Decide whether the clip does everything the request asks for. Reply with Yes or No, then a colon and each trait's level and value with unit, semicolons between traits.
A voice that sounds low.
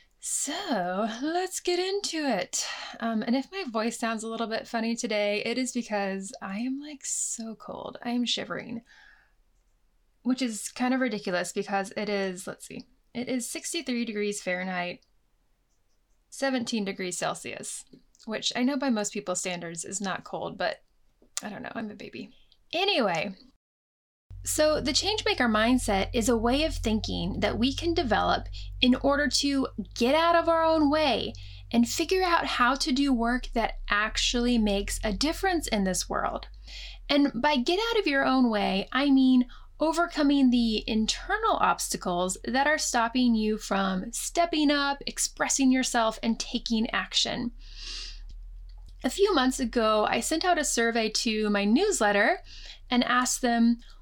No: high, 240 Hz